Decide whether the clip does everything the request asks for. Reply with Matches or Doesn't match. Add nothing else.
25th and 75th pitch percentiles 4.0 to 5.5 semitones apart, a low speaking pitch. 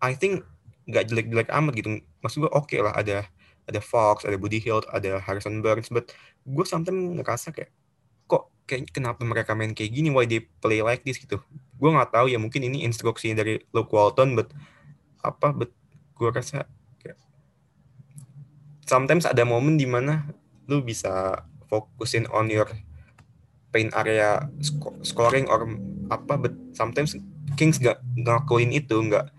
Matches